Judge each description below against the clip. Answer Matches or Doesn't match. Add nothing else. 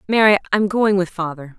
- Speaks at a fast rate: Doesn't match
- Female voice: Matches